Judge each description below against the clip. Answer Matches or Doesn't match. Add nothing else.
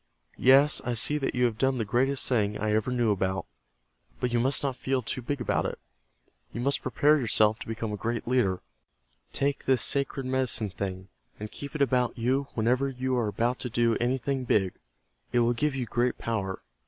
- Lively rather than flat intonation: Doesn't match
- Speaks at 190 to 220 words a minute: Matches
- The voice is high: Doesn't match